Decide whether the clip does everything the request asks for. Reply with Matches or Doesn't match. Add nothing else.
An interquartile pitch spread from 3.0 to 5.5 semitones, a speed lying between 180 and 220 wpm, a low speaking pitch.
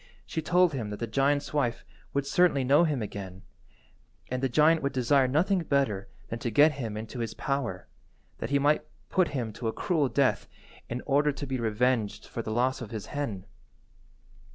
Matches